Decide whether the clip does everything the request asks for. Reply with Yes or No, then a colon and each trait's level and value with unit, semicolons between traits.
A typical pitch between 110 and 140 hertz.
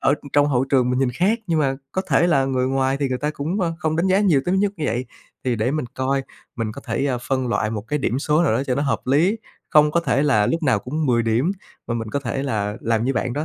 Yes: low, 135 Hz